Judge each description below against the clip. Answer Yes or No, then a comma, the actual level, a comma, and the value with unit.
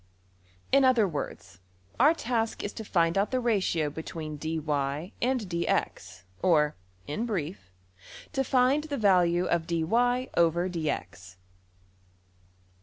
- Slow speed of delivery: Yes, slow, 100 wpm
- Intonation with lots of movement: Yes, wide, 7.3 semitones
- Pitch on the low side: No, medium, 175 Hz